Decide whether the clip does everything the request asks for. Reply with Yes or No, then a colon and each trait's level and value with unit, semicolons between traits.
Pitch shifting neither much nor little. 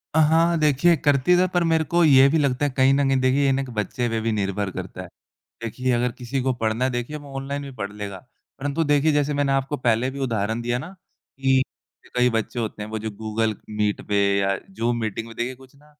Yes: average, 4.0 semitones